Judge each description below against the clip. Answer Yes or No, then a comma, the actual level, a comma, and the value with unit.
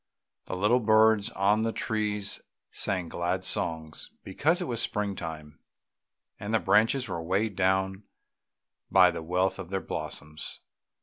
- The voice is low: Yes, low, 100 Hz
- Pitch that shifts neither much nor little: Yes, average, 3.5 semitones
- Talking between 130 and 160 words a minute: Yes, average, 140 wpm